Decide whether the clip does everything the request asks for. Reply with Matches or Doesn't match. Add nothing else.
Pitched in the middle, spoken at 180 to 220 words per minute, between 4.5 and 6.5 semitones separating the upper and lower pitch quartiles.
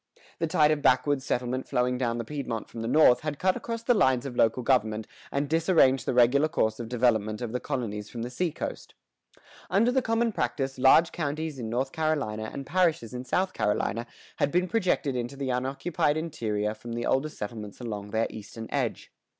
Doesn't match